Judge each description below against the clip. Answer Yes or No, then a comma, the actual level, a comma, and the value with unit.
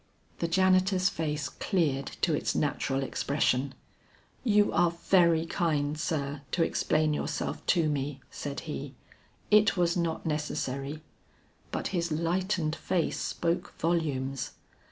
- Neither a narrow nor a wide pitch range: Yes, average, 3.3 semitones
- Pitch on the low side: No, medium, 160 Hz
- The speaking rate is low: Yes, slow, 120 wpm